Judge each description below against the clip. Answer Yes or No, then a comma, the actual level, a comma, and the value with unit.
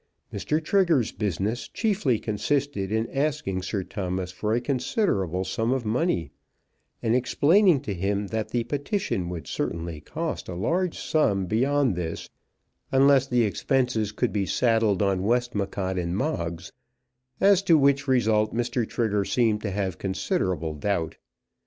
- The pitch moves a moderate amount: No, wide, 6.1 semitones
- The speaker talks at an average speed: Yes, average, 145 wpm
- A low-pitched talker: Yes, low, 110 Hz